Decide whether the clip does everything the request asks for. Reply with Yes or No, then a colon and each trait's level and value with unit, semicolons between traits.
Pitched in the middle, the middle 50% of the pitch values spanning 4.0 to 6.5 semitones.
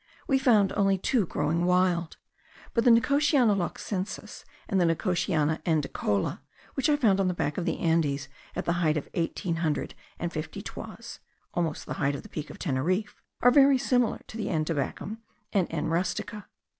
Yes: medium, 180 Hz; wide, 5.5 semitones